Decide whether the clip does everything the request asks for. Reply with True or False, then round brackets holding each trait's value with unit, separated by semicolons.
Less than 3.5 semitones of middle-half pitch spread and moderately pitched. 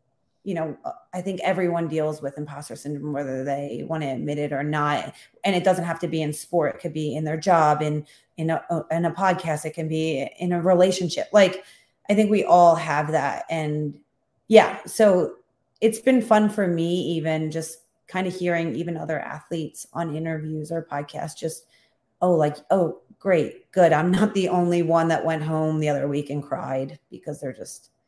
True (2.8 semitones; 160 Hz)